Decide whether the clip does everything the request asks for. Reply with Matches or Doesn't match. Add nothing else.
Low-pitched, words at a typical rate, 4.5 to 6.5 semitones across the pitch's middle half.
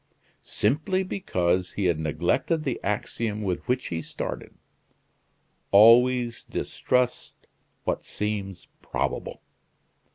Doesn't match